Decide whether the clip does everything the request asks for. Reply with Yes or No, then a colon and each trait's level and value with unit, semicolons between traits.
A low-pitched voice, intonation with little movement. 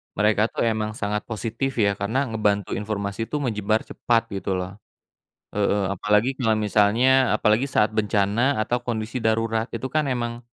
Yes: low, 110 Hz; narrow, 2.3 semitones